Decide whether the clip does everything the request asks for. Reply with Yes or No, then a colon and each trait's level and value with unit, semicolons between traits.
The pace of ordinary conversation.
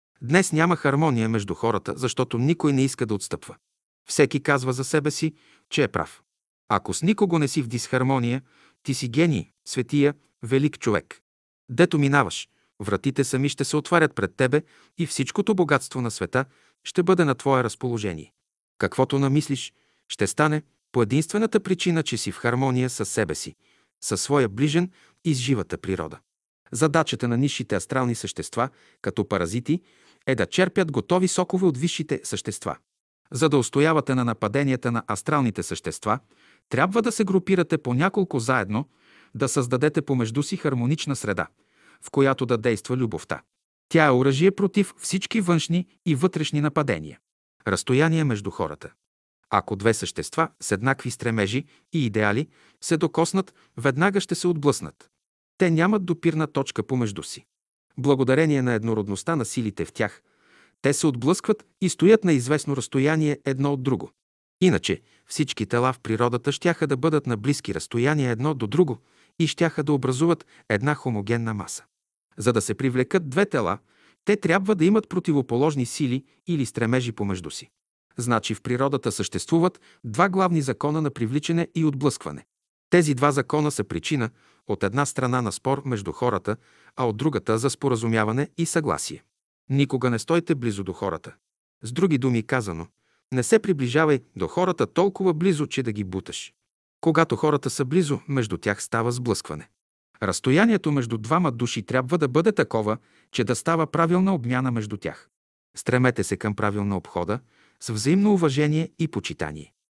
Yes: average, 155 wpm